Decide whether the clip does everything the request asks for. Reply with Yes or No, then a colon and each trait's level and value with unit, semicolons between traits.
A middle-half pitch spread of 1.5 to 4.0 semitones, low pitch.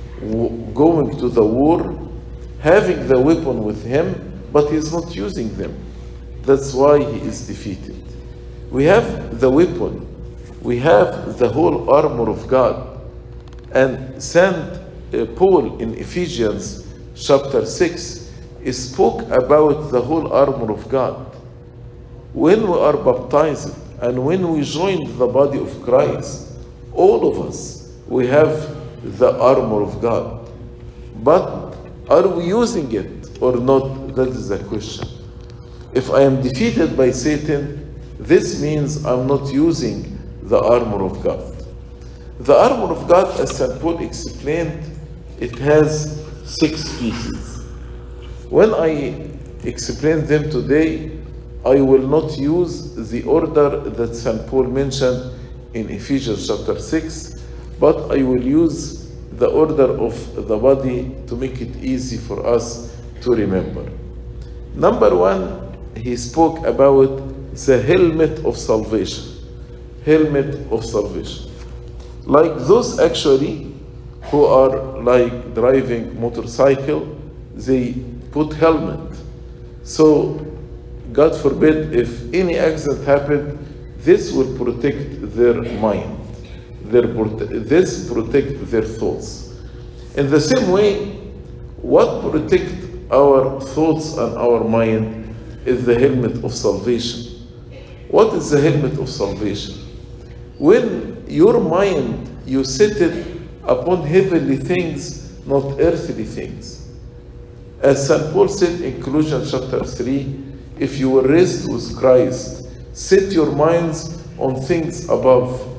No: average, 4.4 semitones; low, 130 Hz